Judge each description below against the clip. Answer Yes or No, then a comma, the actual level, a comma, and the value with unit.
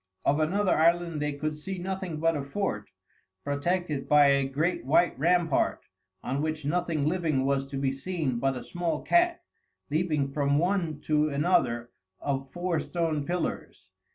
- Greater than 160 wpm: No, average, 155 wpm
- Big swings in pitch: No, average, 3.9 semitones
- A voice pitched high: No, medium, 155 Hz